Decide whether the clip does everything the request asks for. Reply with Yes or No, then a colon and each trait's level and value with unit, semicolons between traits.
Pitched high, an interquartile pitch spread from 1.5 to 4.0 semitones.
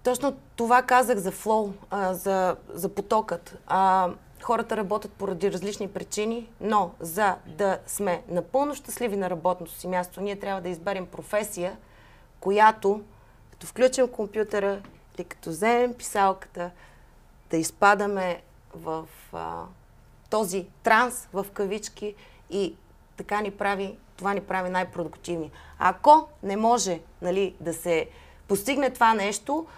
Yes: high, 195 Hz; average, 3.3 semitones